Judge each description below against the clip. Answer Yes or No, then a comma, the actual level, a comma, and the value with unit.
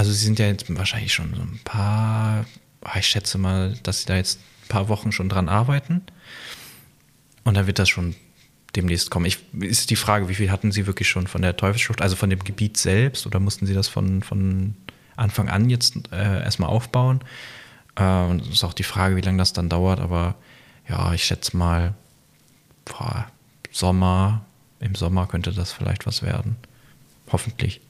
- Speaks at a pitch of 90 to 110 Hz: Yes, low, 100 Hz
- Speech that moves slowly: No, average, 185 wpm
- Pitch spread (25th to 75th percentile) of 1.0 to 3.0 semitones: No, average, 3.4 semitones